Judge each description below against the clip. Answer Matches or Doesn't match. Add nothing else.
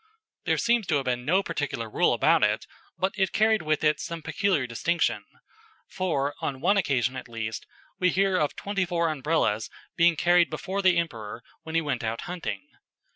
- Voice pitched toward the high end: Doesn't match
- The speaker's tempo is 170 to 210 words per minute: Matches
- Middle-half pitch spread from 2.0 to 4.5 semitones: Doesn't match